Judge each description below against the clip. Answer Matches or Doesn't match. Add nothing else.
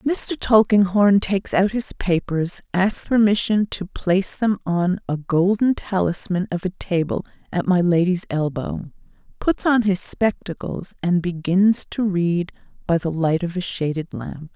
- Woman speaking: Matches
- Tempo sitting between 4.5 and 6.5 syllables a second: Doesn't match